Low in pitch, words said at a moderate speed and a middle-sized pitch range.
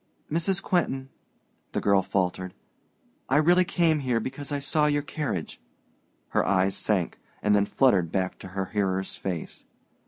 No: low, 115 Hz; average, 150 wpm; wide, 7.7 semitones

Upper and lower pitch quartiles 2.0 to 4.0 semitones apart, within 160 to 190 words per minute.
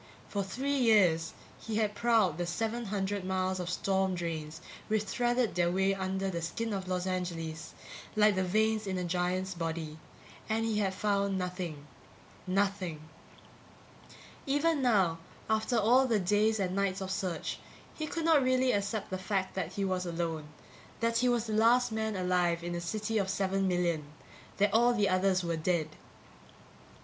Yes: average, 3.5 semitones; average, 170 wpm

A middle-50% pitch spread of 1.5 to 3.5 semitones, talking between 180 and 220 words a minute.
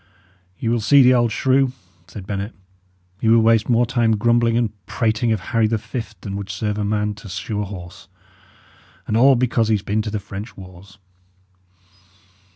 Yes: narrow, 2.5 semitones; average, 185 wpm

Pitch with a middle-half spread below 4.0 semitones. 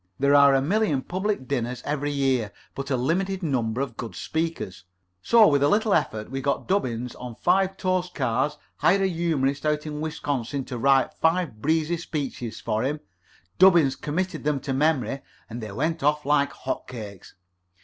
No: average, 4.3 semitones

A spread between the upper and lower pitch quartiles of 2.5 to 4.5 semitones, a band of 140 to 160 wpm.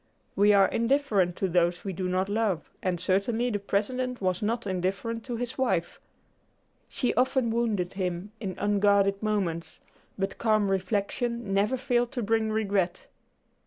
Yes: average, 3.6 semitones; average, 150 wpm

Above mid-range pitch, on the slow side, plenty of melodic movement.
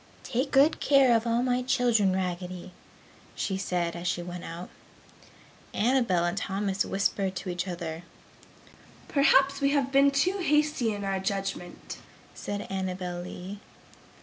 Yes: high, 195 Hz; slow, 130 wpm; wide, 6.3 semitones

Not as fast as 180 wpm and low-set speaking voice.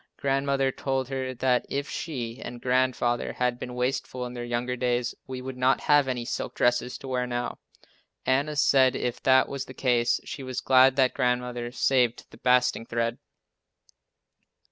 Yes: average, 165 wpm; low, 125 Hz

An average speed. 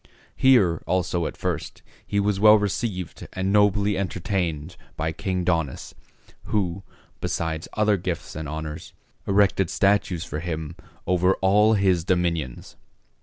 No: slow, 125 wpm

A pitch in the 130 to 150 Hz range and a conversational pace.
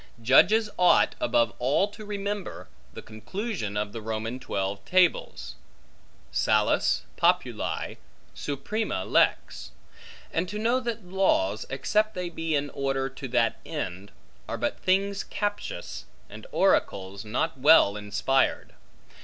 No: low, 135 Hz; slow, 120 wpm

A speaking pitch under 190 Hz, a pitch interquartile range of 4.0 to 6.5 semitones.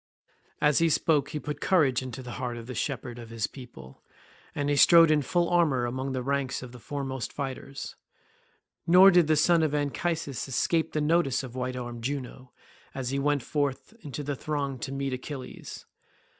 No: medium, 140 Hz; average, 2.9 semitones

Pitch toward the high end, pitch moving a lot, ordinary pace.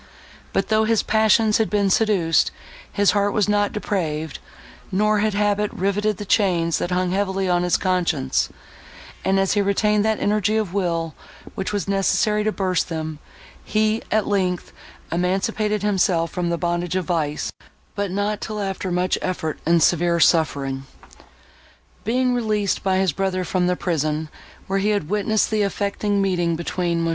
No: high, 195 Hz; average, 3.2 semitones; average, 165 wpm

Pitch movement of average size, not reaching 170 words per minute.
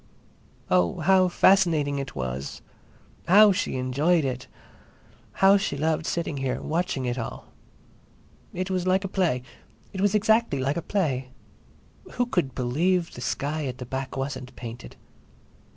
No: wide, 6.4 semitones; average, 145 wpm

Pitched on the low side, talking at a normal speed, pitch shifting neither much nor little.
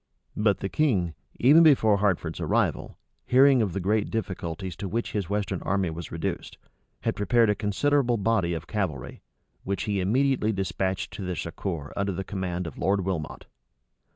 Yes: low, 100 Hz; average, 165 wpm; average, 3.4 semitones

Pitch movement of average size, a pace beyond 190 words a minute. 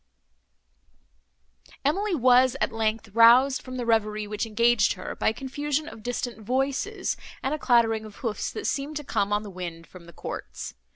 No: average, 4.0 semitones; average, 175 wpm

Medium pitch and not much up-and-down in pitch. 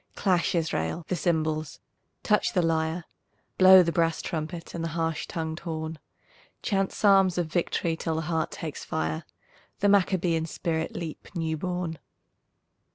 Yes: medium, 165 Hz; narrow, 2.0 semitones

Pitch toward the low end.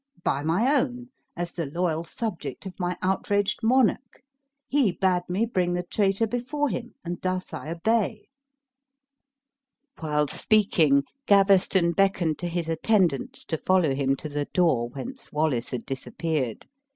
No: medium, 180 Hz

